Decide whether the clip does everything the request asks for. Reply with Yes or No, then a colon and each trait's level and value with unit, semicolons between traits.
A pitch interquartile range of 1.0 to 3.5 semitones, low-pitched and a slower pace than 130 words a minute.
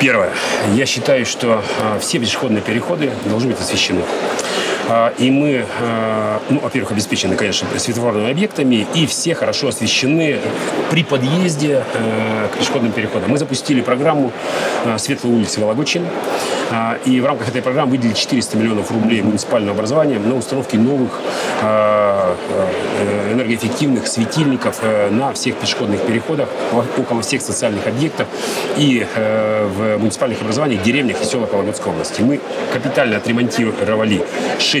Yes: average, 3.2 semitones; low, 115 Hz; average, 120 wpm